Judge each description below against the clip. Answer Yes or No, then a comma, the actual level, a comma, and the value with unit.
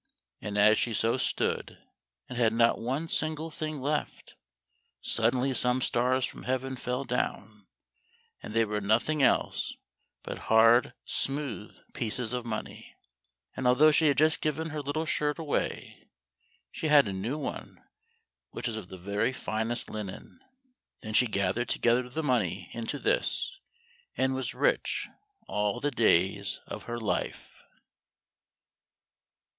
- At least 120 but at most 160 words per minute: Yes, average, 140 wpm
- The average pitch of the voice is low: Yes, low, 125 Hz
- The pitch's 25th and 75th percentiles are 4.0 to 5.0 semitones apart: Yes, average, 4.7 semitones